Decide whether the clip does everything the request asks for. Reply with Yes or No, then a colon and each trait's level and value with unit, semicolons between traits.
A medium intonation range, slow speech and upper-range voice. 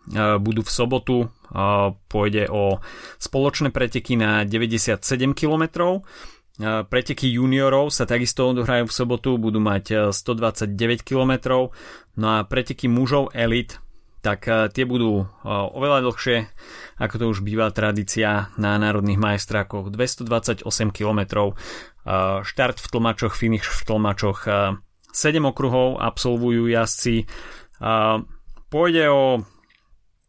No: average, 3.5 semitones; slow, 105 wpm; low, 115 Hz